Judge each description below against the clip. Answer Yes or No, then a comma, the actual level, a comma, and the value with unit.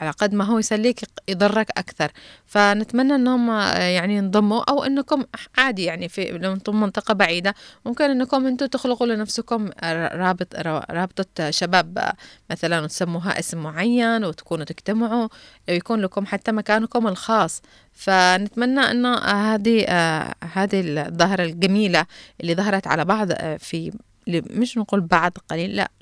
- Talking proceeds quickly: No, average, 125 wpm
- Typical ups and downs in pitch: Yes, average, 4.4 semitones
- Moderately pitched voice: No, high, 200 Hz